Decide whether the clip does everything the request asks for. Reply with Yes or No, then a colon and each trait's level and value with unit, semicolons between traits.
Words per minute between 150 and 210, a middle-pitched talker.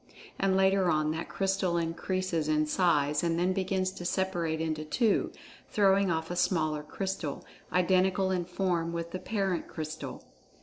Yes: average, 155 wpm; medium, 175 Hz